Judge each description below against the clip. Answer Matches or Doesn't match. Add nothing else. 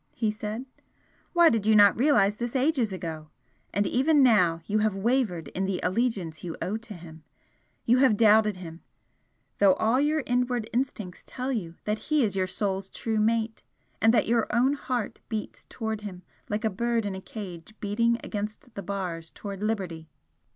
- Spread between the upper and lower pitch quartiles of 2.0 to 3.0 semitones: Doesn't match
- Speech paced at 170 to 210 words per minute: Matches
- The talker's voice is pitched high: Matches